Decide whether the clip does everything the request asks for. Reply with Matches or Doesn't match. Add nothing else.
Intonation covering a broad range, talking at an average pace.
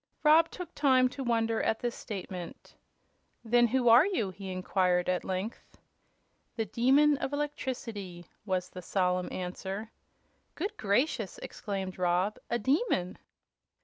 Doesn't match